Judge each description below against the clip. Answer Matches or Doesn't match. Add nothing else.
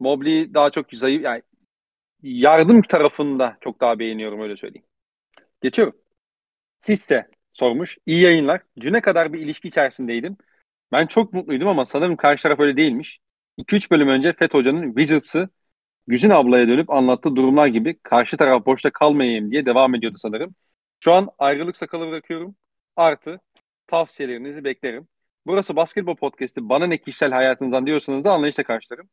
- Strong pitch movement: Doesn't match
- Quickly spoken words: Matches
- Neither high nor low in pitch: Matches